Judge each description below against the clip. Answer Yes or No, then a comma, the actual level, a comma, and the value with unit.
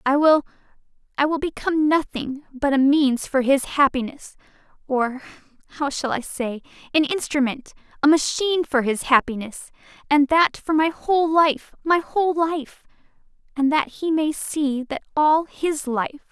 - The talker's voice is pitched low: No, very high, 290 Hz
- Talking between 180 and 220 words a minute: No, average, 145 wpm